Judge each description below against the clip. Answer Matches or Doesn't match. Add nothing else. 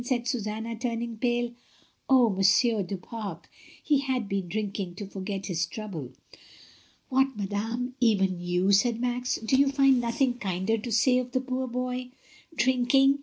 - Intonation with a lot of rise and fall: Doesn't match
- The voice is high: Matches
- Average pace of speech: Matches